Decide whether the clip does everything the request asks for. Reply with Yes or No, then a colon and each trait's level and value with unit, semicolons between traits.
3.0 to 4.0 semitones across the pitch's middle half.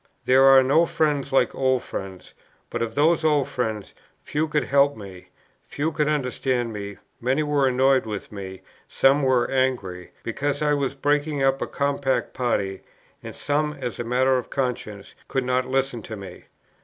Yes: average, 3.5 semitones